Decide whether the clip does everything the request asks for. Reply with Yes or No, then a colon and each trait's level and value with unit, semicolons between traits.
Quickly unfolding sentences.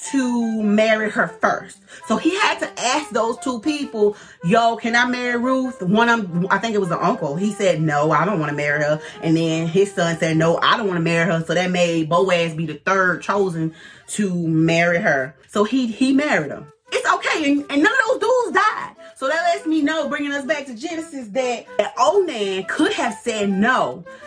Yes: fast, 225 wpm